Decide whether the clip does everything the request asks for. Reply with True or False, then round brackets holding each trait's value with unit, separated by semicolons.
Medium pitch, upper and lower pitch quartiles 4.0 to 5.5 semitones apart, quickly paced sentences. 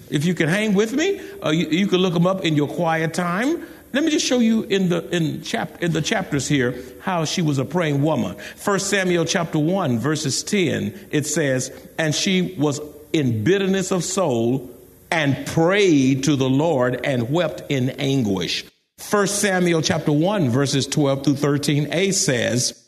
False (160 Hz; 5.1 semitones; 185 wpm)